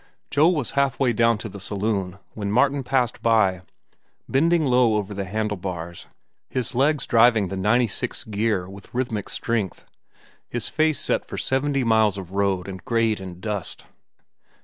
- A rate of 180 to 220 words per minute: No, average, 160 wpm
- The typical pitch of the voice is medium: No, low, 110 Hz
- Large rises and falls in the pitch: No, average, 4.3 semitones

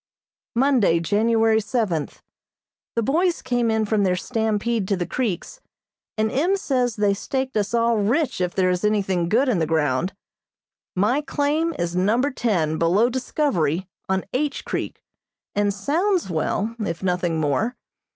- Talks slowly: No, average, 150 wpm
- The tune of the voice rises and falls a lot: Yes, wide, 5.7 semitones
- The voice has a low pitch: No, high, 215 Hz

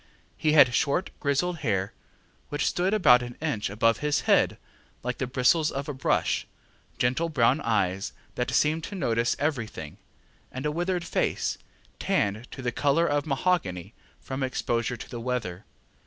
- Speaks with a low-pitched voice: Yes, low, 130 Hz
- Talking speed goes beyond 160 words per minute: No, average, 155 wpm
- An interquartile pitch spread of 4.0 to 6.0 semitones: Yes, average, 4.8 semitones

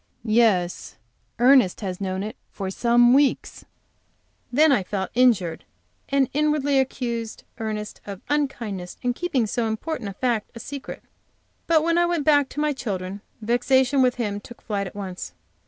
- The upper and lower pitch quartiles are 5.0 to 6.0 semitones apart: Yes, wide, 5.4 semitones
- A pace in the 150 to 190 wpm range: Yes, average, 155 wpm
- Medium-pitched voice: No, high, 240 Hz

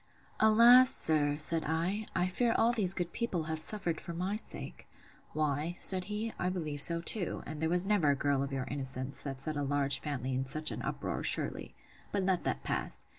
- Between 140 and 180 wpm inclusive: No, average, 195 wpm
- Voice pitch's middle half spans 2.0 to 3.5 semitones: No, average, 5.0 semitones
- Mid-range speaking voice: Yes, medium, 165 Hz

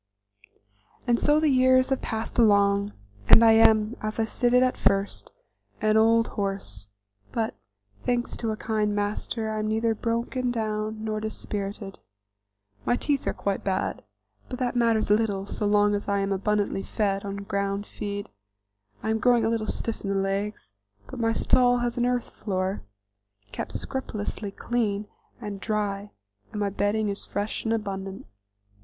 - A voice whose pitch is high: Yes, high, 215 Hz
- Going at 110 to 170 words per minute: Yes, average, 160 wpm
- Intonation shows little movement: Yes, narrow, 2.3 semitones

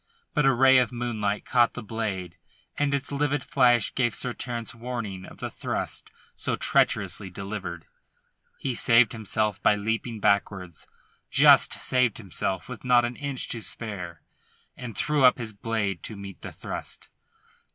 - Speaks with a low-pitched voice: Yes, low, 115 Hz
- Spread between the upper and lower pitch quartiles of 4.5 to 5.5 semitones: No, average, 3.8 semitones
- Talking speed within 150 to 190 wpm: Yes, average, 155 wpm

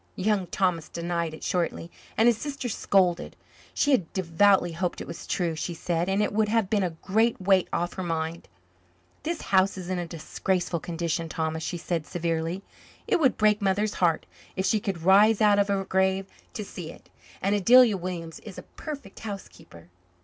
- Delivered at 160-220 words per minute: Yes, average, 185 wpm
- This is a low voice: No, medium, 185 Hz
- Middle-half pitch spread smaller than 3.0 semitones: No, average, 3.4 semitones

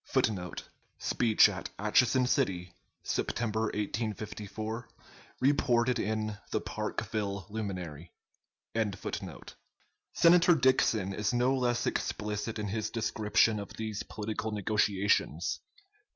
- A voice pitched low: Yes, low, 110 Hz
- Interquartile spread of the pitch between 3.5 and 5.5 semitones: No, narrow, 2.6 semitones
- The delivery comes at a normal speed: No, slow, 95 wpm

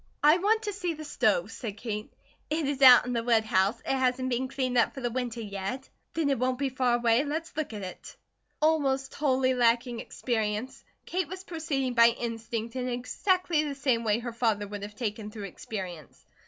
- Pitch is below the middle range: No, very high, 250 Hz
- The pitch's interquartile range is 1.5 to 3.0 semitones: No, average, 3.8 semitones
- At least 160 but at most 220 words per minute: Yes, average, 195 wpm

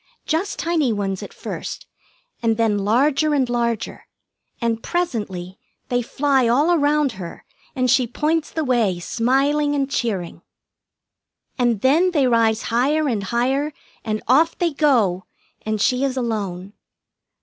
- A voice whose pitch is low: No, high, 245 Hz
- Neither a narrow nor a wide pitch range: Yes, average, 4.8 semitones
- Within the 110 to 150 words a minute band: Yes, average, 140 wpm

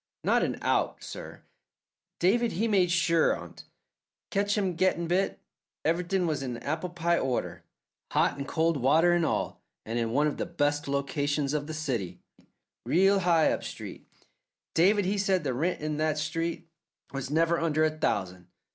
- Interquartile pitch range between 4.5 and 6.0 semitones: No, average, 3.6 semitones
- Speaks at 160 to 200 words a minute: Yes, average, 165 wpm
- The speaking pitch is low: No, medium, 160 Hz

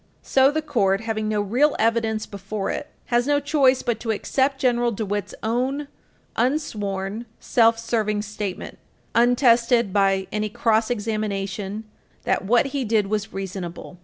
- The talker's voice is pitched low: No, high, 220 Hz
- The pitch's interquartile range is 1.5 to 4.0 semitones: Yes, average, 3.1 semitones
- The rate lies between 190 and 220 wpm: No, average, 140 wpm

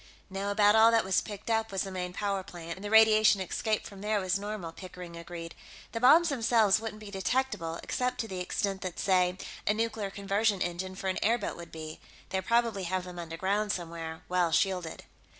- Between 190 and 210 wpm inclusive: Yes, average, 200 wpm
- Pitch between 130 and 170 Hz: No, high, 195 Hz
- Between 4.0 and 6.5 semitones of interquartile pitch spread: No, average, 3.2 semitones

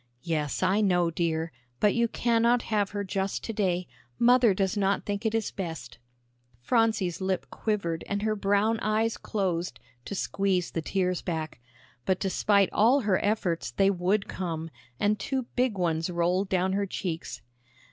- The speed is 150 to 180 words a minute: Yes, average, 160 wpm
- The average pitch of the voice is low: No, high, 195 Hz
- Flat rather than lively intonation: No, average, 3.2 semitones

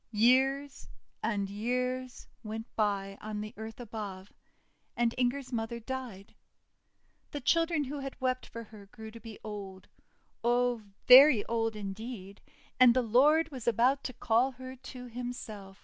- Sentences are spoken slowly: No, average, 150 wpm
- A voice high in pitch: Yes, high, 235 Hz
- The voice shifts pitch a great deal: No, average, 3.2 semitones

